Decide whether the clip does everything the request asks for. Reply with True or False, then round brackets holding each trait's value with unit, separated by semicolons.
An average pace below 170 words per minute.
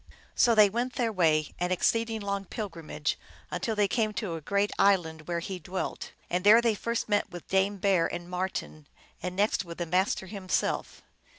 False (185 wpm)